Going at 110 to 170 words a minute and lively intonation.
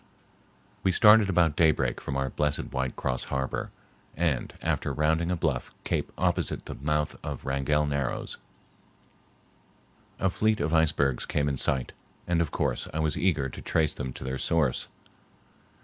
No: average, 155 wpm; average, 3.5 semitones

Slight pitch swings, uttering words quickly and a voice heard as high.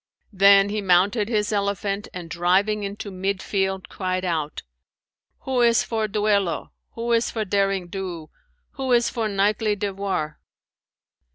No: narrow, 2.2 semitones; average, 140 wpm; high, 200 Hz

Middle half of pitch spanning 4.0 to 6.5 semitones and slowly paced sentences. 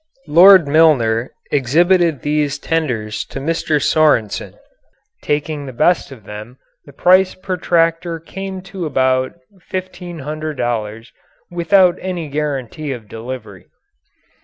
Yes: average, 5.1 semitones; slow, 110 wpm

